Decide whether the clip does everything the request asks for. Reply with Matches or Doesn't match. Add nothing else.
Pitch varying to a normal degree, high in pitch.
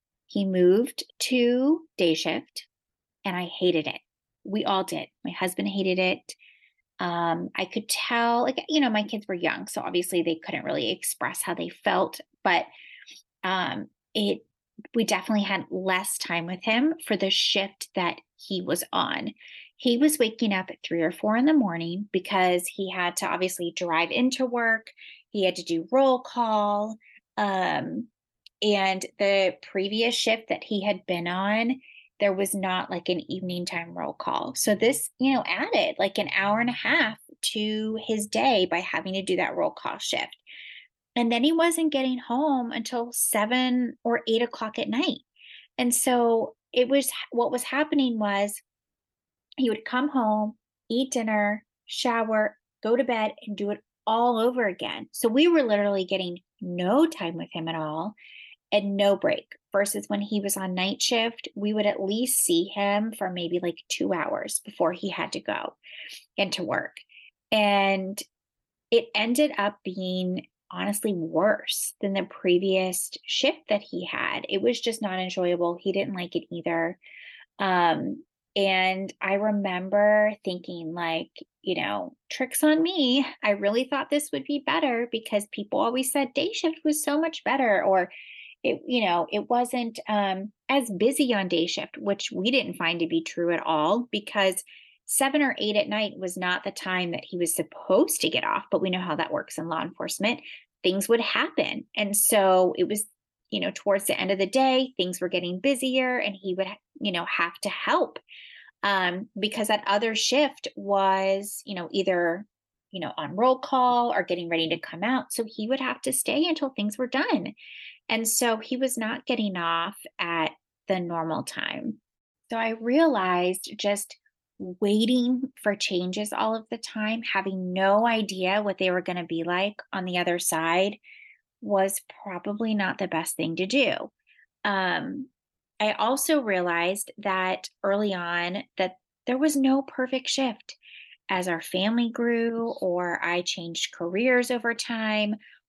Matches